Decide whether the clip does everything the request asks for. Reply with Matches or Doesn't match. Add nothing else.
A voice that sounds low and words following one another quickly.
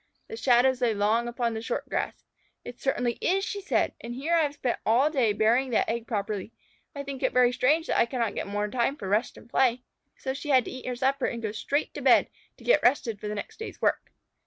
Doesn't match